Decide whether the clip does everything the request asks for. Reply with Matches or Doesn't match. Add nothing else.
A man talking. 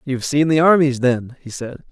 Matches